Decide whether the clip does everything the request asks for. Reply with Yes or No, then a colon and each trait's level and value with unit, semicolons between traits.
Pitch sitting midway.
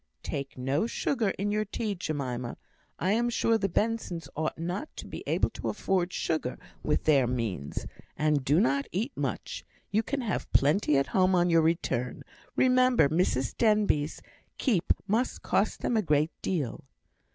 Yes: medium, 175 Hz